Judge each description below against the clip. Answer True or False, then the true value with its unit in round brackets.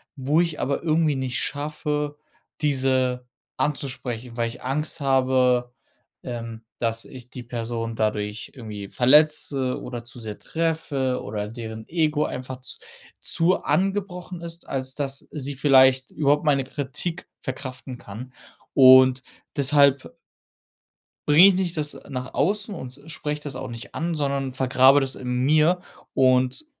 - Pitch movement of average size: True (3.1 semitones)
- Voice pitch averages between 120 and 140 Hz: True (135 Hz)